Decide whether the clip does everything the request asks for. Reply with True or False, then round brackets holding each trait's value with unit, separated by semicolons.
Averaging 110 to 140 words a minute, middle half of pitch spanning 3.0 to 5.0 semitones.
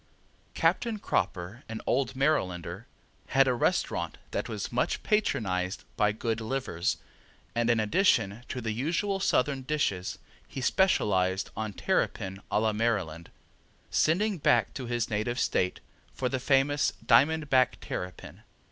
False (135 wpm; 5.4 semitones)